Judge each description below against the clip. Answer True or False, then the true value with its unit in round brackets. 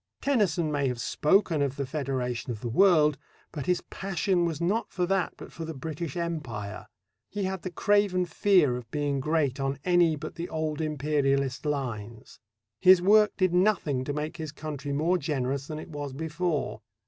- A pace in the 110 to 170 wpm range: False (180 wpm)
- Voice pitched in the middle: True (155 Hz)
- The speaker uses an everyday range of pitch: True (4.3 semitones)